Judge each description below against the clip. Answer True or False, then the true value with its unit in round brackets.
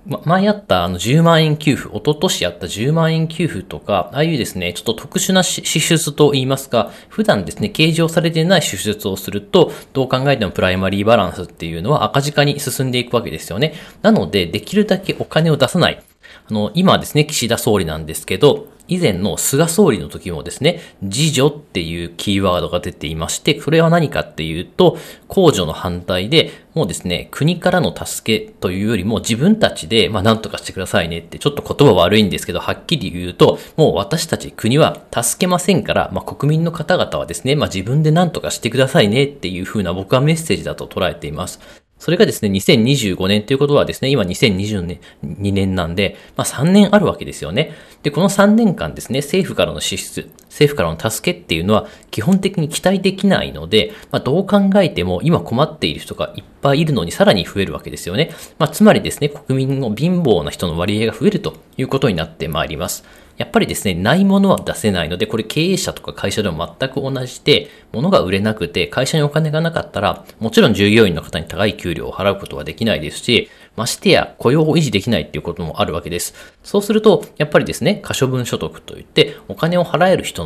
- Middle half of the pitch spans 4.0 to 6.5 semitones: False (8.7 semitones)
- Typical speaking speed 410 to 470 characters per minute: True (425 characters per minute)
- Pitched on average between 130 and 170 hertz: True (135 Hz)